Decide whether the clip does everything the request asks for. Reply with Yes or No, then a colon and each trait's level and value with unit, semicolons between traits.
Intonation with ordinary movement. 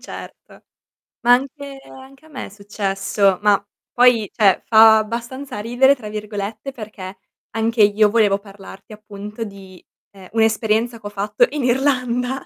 Yes: average, 3.3 semitones